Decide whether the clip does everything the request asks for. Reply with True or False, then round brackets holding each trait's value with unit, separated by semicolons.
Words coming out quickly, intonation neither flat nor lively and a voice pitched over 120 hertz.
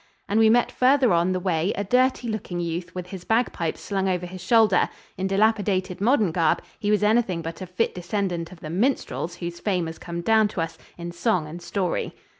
True (210 wpm; 3.9 semitones; 185 Hz)